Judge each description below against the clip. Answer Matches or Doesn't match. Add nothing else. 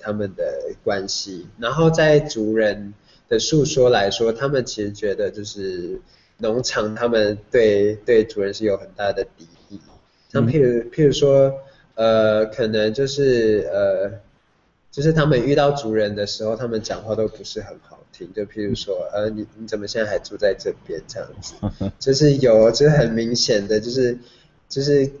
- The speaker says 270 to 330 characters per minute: Doesn't match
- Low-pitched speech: Matches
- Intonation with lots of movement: Doesn't match